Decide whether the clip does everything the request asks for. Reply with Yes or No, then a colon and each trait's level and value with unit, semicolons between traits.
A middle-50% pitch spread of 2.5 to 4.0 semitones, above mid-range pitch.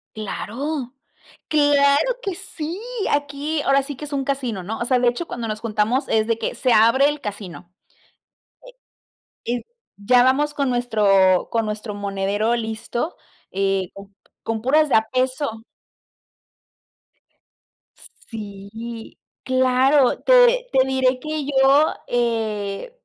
No: average, 4.6 semitones; high, 245 Hz